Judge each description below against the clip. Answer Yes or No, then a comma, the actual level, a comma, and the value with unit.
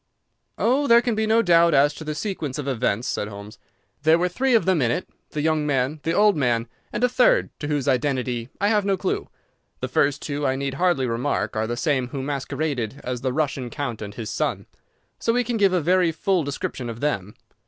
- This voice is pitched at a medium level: Yes, medium, 145 Hz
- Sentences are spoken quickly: Yes, fast, 225 wpm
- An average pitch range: No, wide, 6.3 semitones